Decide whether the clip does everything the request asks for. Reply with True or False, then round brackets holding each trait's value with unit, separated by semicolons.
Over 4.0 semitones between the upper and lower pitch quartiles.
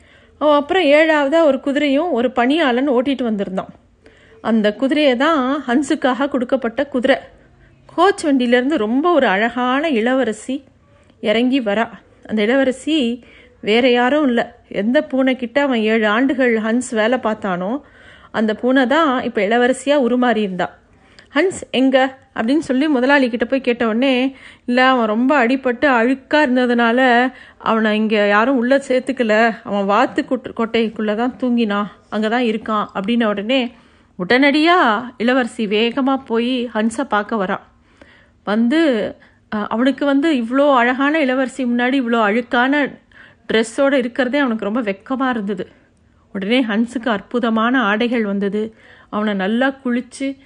False (3.3 semitones)